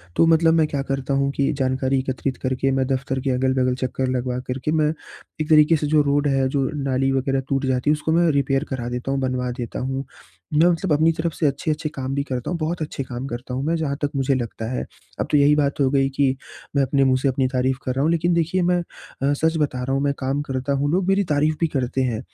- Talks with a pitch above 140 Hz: No, low, 135 Hz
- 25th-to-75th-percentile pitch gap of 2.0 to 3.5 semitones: Yes, narrow, 2.6 semitones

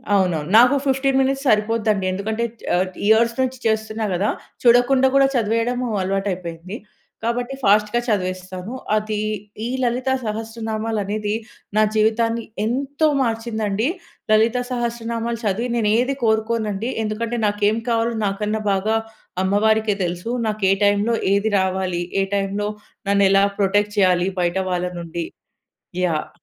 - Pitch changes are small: No, average, 3.0 semitones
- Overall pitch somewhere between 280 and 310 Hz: No, high, 215 Hz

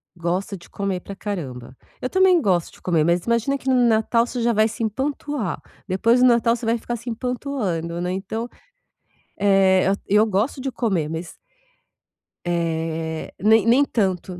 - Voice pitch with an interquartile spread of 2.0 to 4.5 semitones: No, average, 5.1 semitones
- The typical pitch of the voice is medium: No, high, 210 Hz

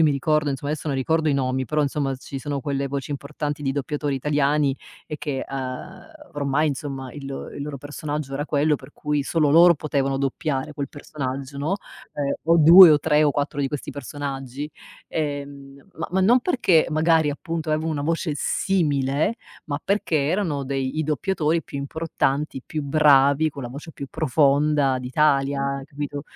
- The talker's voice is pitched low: No, medium, 145 Hz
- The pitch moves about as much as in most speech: No, narrow, 2.0 semitones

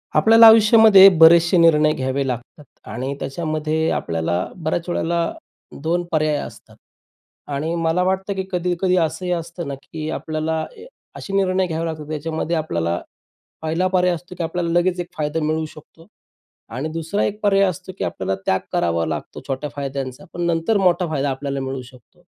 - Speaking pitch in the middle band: Yes, medium, 160 Hz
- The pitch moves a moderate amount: Yes, average, 4.0 semitones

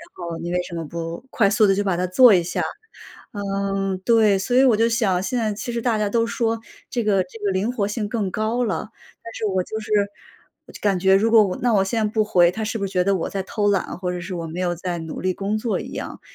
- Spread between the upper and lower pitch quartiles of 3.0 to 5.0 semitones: Yes, average, 3.4 semitones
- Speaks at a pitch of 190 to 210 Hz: Yes, high, 200 Hz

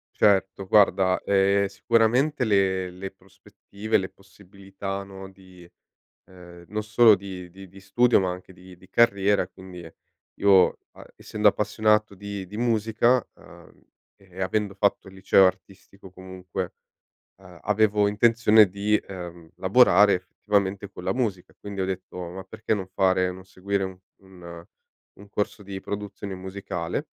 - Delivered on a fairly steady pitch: Yes, narrow, 1.8 semitones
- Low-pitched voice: Yes, very low, 95 Hz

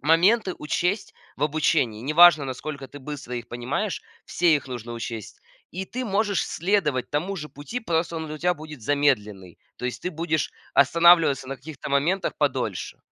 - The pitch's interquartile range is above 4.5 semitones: Yes, average, 4.9 semitones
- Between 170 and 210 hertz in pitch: No, medium, 150 Hz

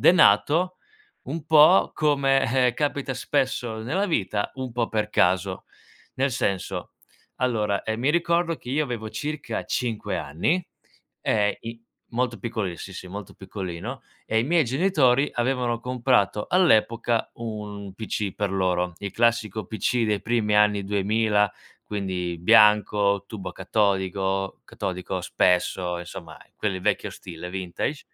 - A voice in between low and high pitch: No, low, 110 Hz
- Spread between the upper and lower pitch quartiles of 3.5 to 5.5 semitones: Yes, average, 4.7 semitones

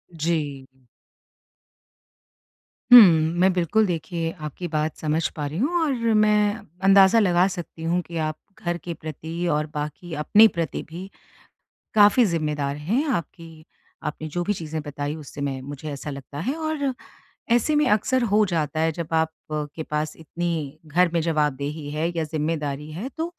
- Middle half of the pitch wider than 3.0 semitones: Yes, average, 3.9 semitones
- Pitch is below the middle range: No, medium, 165 Hz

